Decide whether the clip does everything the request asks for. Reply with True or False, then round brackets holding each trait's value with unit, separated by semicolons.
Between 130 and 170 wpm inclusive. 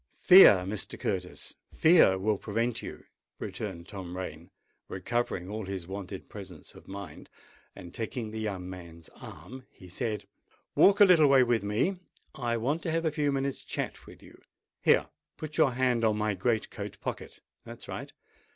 True (160 wpm)